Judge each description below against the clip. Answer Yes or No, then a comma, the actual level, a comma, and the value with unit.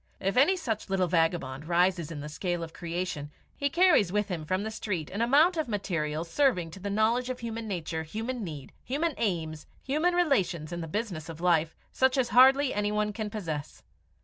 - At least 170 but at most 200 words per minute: Yes, average, 195 wpm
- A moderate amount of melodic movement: No, wide, 6.6 semitones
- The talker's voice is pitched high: Yes, high, 195 Hz